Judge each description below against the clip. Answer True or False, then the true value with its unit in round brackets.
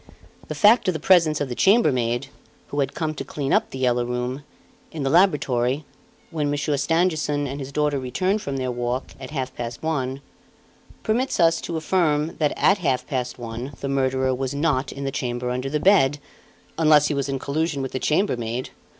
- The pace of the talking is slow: False (195 wpm)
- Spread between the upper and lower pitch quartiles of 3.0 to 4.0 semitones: True (3.5 semitones)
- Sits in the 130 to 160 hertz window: True (140 Hz)